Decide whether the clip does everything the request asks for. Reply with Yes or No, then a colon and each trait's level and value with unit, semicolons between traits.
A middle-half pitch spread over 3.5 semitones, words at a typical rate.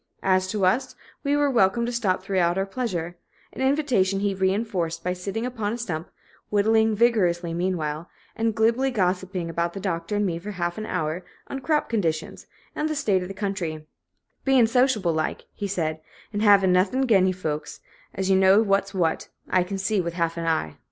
Yes: average, 4.2 semitones; average, 190 wpm